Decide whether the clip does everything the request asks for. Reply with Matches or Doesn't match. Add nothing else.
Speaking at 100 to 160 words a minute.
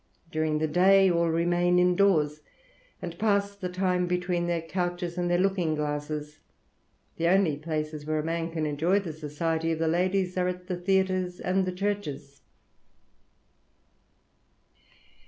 Matches